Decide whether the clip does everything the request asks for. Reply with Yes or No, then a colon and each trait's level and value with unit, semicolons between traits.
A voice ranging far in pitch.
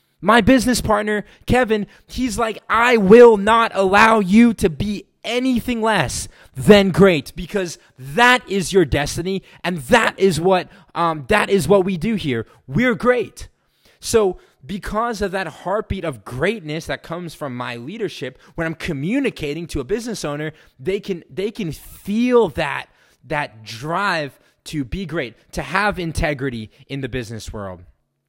Yes: wide, 6.7 semitones